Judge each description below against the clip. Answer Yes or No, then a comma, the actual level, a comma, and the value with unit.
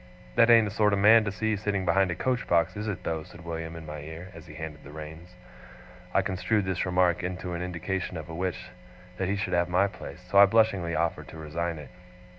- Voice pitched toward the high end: No, very low, 90 Hz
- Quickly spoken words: Yes, fast, 235 wpm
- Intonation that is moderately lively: Yes, average, 3.3 semitones